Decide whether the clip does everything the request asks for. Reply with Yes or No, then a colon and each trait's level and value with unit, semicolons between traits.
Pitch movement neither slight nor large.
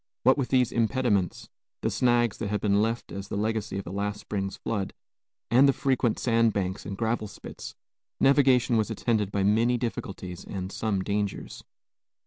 Yes: average, 3.2 semitones